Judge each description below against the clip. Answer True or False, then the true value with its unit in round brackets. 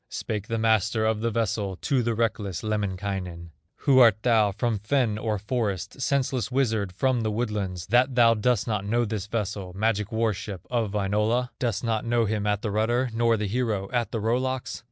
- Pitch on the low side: True (110 Hz)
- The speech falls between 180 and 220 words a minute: True (195 wpm)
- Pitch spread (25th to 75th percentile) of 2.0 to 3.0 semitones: True (2.6 semitones)